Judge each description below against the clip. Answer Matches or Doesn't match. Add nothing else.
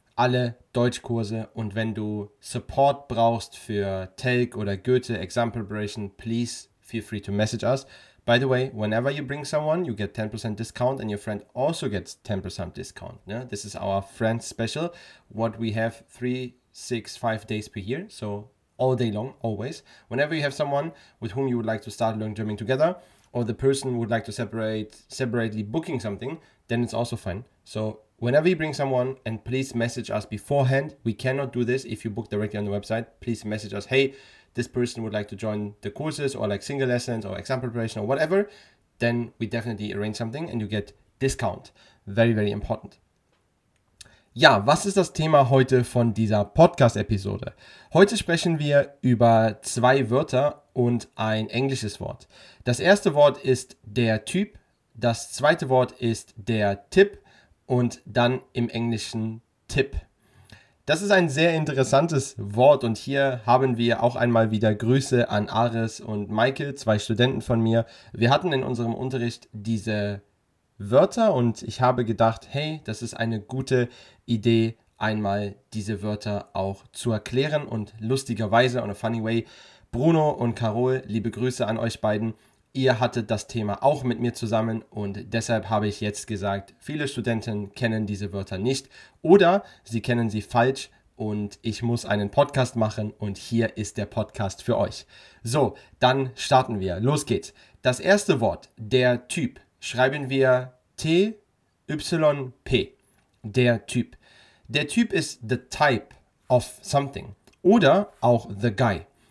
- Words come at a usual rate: Matches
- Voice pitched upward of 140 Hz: Doesn't match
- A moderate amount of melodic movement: Matches